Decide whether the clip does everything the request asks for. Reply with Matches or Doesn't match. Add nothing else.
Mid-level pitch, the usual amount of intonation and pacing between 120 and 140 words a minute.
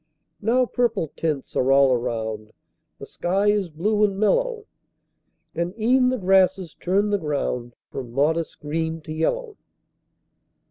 Doesn't match